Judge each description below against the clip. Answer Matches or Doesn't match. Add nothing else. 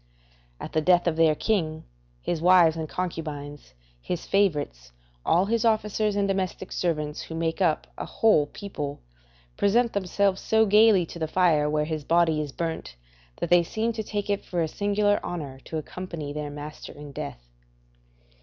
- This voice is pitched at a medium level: Matches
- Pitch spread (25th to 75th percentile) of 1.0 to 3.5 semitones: Doesn't match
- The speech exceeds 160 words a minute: Matches